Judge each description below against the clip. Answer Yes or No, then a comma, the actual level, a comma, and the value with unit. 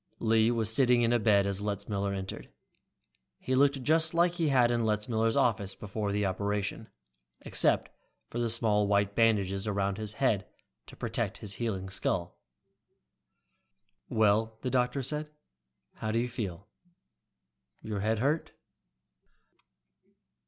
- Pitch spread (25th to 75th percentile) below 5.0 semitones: Yes, average, 3.1 semitones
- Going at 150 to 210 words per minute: No, slow, 135 wpm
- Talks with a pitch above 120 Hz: No, low, 110 Hz